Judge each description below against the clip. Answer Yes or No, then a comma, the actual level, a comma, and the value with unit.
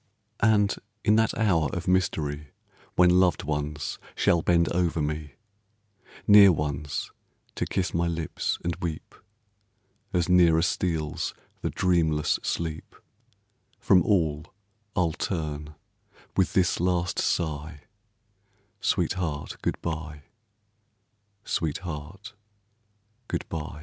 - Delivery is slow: Yes, slow, 105 wpm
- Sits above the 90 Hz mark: No, very low, 85 Hz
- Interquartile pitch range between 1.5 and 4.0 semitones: Yes, average, 3.0 semitones